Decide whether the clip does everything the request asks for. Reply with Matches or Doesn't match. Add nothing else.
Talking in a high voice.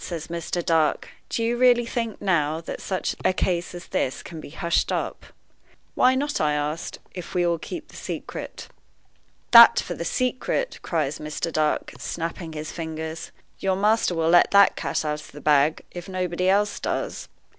Doesn't match